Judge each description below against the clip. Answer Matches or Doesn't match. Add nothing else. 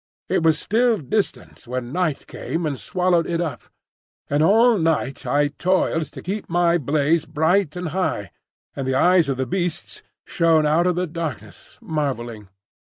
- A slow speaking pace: Doesn't match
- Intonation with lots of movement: Doesn't match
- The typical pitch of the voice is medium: Matches